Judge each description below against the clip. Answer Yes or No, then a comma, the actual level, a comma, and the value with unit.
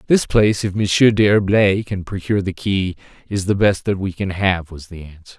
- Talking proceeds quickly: Yes, fast, 210 wpm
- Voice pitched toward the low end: Yes, very low, 95 Hz